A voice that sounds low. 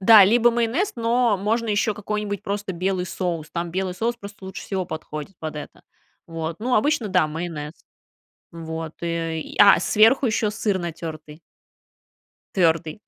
No: high, 190 Hz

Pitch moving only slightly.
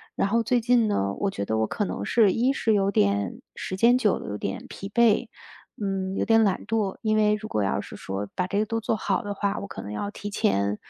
No: average, 3.6 semitones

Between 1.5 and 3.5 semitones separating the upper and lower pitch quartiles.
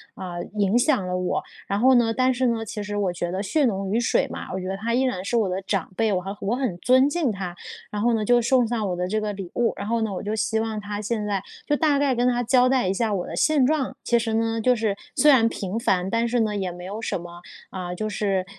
No: average, 3.9 semitones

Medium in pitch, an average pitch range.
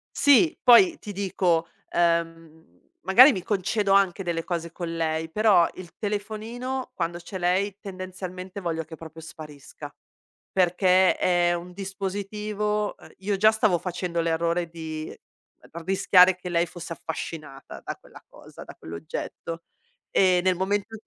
Yes: medium, 180 Hz; average, 3.1 semitones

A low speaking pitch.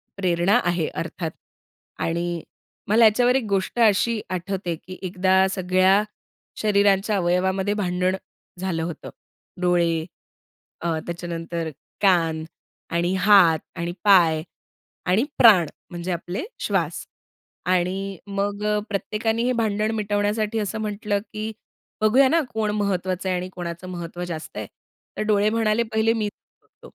No: high, 190 Hz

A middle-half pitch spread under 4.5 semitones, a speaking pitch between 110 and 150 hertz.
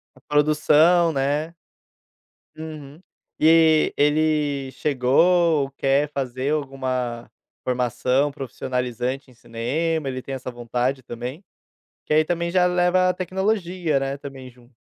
Yes: average, 3.8 semitones; medium, 140 Hz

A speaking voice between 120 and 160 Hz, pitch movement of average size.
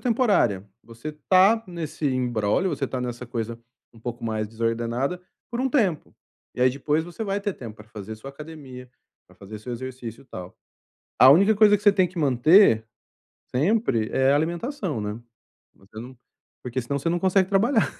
No: low, 135 Hz; wide, 8.2 semitones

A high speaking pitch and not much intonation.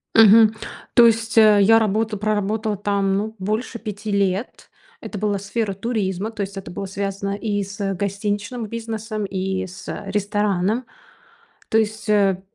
Yes: high, 205 Hz; narrow, 1.8 semitones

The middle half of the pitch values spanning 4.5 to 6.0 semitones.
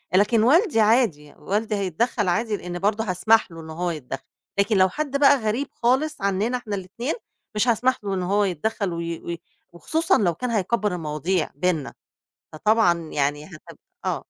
Yes: average, 4.9 semitones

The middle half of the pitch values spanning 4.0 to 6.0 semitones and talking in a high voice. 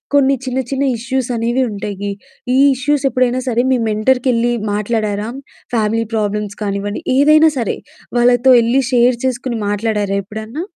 No: average, 3.6 semitones; high, 235 Hz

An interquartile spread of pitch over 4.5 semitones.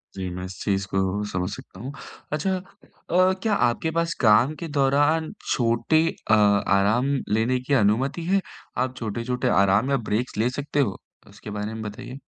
Yes: average, 5.2 semitones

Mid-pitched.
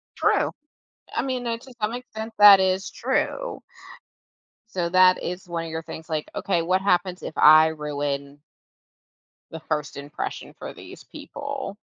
Yes: medium, 180 Hz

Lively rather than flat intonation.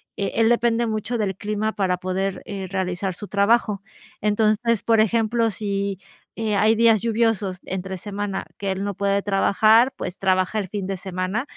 No: narrow, 2.5 semitones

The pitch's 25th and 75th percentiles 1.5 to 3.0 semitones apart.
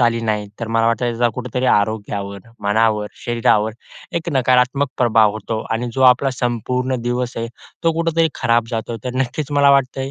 Yes: narrow, 2.6 semitones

